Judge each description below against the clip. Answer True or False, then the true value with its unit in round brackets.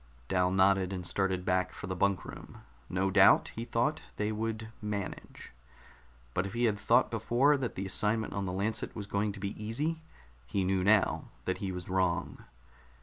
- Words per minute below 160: False (185 wpm)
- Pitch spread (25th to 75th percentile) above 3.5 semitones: False (3.0 semitones)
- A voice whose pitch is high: False (100 Hz)